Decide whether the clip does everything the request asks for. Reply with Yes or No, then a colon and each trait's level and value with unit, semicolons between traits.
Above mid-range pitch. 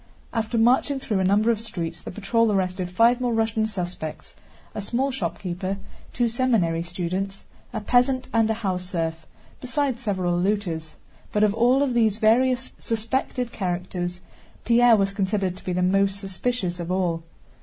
Yes: high, 205 Hz